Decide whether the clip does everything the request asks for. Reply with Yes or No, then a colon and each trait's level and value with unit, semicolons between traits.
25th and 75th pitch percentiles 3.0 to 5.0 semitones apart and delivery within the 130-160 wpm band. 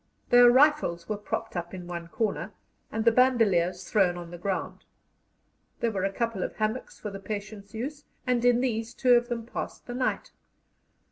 No: average, 4.3 semitones; average, 185 wpm